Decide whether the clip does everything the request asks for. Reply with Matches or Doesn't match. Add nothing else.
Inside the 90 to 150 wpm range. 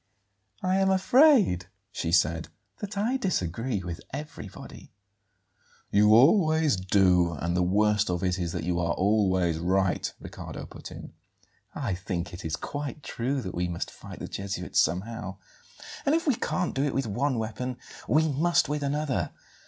Doesn't match